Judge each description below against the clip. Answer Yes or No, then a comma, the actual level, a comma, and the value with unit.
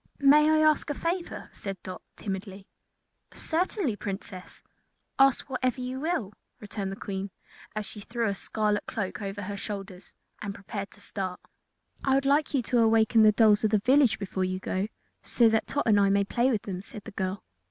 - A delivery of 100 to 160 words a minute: No, average, 190 wpm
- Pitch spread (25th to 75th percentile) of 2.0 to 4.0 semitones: No, average, 4.5 semitones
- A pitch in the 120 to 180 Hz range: No, high, 210 Hz